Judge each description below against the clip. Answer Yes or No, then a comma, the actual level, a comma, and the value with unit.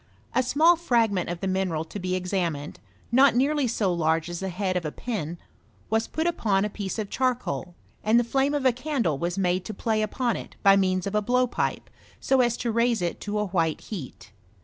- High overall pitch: Yes, high, 205 Hz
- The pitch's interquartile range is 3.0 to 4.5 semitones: No, average, 5.3 semitones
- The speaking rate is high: Yes, fast, 215 wpm